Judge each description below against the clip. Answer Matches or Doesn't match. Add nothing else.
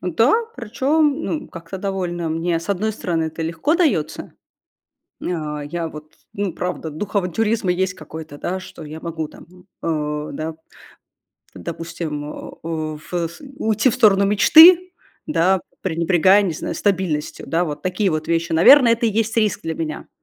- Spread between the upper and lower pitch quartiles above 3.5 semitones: Matches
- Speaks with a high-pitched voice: Doesn't match